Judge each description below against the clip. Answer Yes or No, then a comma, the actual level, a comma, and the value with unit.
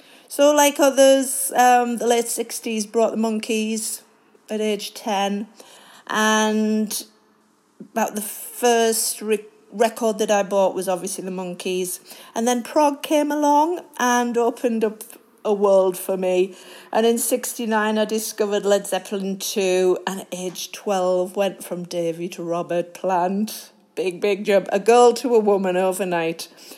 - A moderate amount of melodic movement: Yes, average, 3.7 semitones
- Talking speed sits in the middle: Yes, average, 145 wpm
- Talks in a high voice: Yes, high, 215 Hz